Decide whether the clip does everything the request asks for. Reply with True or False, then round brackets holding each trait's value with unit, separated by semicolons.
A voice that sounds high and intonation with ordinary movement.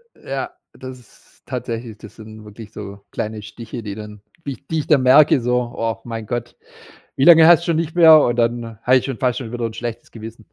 False (120 Hz; 3.3 semitones)